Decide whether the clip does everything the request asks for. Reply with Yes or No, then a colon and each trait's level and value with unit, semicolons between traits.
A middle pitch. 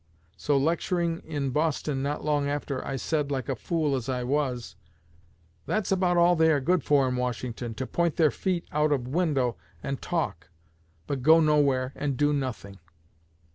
Yes: medium, 145 Hz